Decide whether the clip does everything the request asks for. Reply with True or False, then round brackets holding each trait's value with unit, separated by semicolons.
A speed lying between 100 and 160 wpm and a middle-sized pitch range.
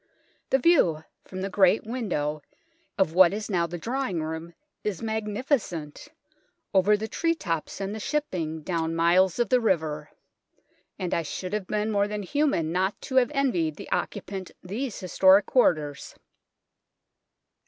True (150 wpm; 4.7 semitones)